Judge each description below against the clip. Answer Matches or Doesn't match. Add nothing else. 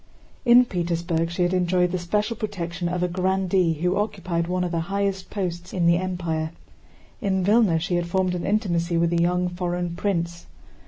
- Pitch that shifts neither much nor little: Doesn't match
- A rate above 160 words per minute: Matches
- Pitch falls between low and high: Matches